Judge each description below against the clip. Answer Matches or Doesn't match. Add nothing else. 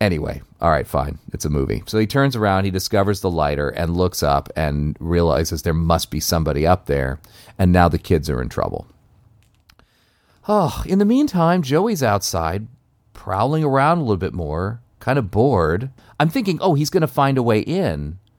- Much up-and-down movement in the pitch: Matches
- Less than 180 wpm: Doesn't match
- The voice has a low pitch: Matches